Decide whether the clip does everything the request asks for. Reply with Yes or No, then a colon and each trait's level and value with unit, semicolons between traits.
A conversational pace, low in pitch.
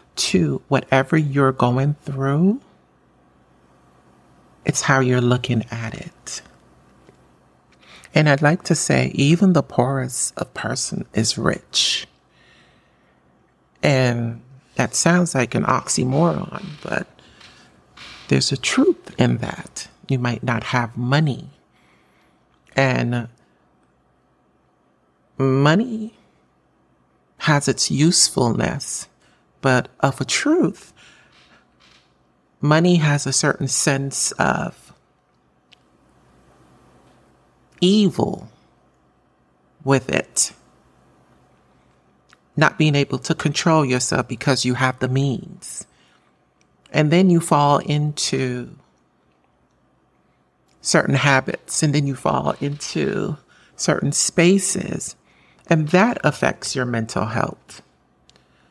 No: slow, 90 wpm; low, 125 Hz